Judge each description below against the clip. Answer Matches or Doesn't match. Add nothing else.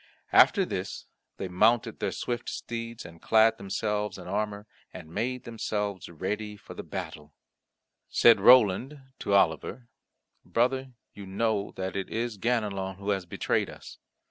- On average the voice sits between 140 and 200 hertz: Doesn't match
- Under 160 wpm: Matches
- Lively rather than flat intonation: Doesn't match